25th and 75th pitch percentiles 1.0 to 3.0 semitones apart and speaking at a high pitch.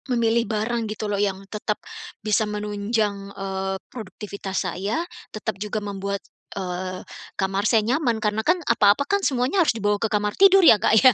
Yes: average, 2.7 semitones; high, 210 Hz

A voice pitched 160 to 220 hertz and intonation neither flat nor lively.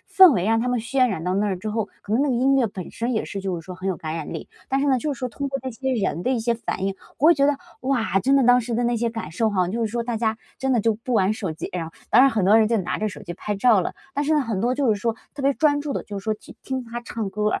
No: high, 230 Hz; average, 4.5 semitones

